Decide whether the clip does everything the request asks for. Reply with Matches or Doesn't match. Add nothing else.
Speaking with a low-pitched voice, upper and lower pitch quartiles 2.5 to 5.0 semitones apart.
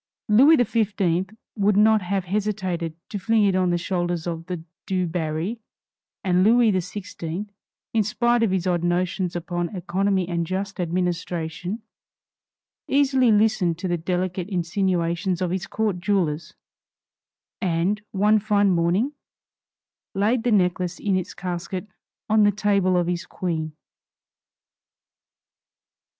Doesn't match